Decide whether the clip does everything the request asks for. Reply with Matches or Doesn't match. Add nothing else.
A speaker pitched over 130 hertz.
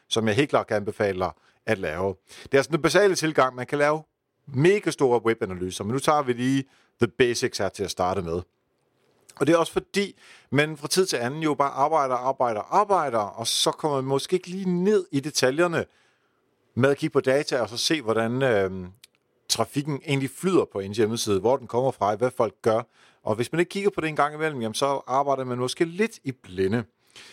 Matches